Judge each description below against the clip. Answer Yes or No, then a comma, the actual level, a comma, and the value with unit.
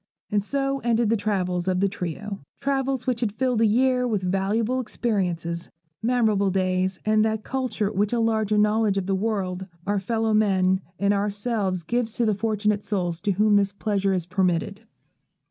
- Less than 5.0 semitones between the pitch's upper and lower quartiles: Yes, average, 2.9 semitones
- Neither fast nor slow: Yes, average, 175 wpm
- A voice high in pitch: Yes, high, 210 Hz